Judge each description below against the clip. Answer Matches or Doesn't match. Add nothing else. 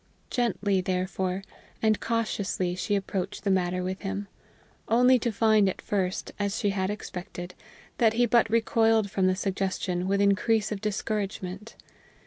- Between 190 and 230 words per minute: Doesn't match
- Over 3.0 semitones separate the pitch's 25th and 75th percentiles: Doesn't match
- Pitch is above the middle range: Matches